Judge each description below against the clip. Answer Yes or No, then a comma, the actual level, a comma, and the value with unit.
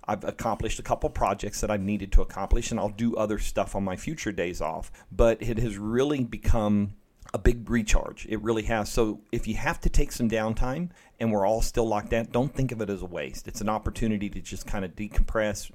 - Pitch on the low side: Yes, low, 110 Hz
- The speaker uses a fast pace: Yes, fast, 230 wpm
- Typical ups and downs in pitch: No, narrow, 2.3 semitones